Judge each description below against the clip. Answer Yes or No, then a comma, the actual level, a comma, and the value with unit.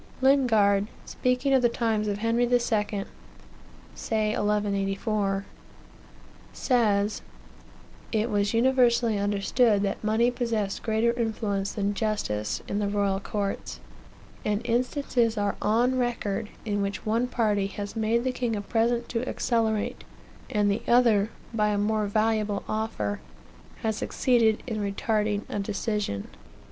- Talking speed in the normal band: No, slow, 130 wpm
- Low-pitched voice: No, high, 215 Hz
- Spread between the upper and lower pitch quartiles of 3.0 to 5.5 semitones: No, narrow, 2.5 semitones